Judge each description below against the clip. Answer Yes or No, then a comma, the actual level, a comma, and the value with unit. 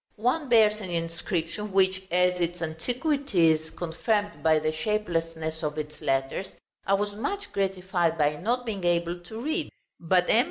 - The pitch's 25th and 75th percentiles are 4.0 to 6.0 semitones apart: Yes, average, 4.4 semitones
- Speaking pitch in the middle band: Yes, medium, 180 Hz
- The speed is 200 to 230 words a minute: No, average, 160 wpm